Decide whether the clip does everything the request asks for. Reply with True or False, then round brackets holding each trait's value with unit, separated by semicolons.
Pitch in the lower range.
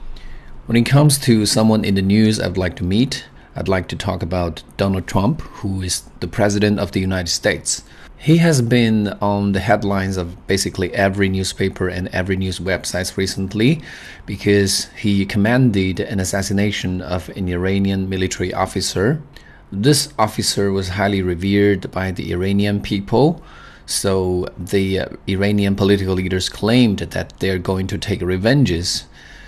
True (95 Hz)